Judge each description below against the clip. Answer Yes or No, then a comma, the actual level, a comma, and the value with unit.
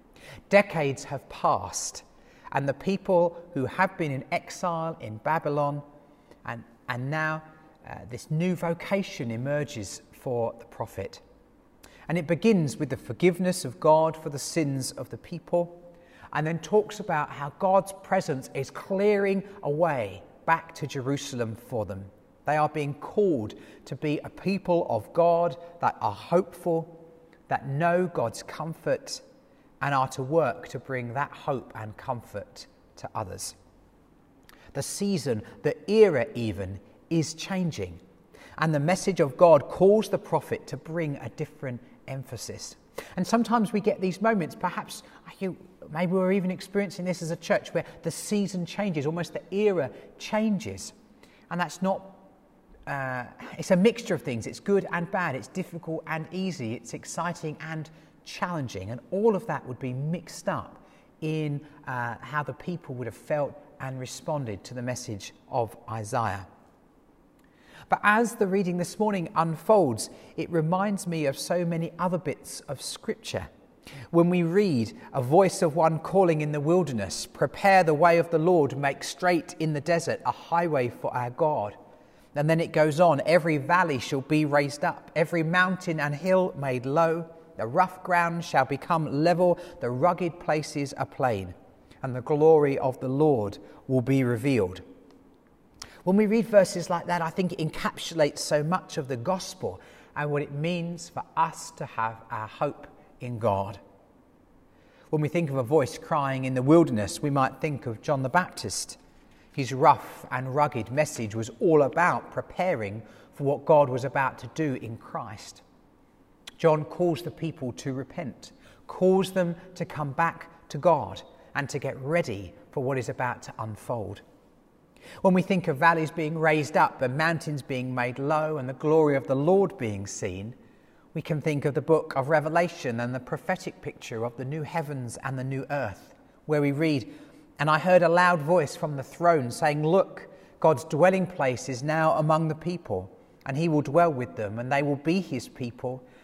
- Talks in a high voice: No, medium, 155 Hz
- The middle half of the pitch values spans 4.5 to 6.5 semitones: Yes, average, 4.8 semitones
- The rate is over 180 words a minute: No, average, 170 wpm